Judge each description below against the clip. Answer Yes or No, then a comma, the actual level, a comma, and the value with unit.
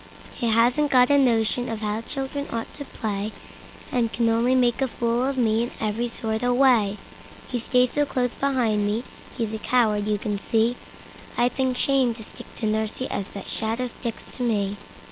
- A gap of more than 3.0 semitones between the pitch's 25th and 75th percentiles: No, narrow, 2.4 semitones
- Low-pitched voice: No, high, 235 Hz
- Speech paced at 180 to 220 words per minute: Yes, average, 185 wpm